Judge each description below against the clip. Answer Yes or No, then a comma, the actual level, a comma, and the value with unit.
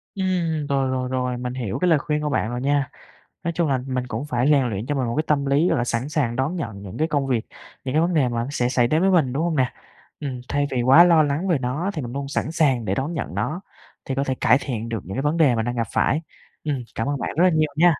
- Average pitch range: Yes, average, 3.8 semitones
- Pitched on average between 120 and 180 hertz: Yes, medium, 140 Hz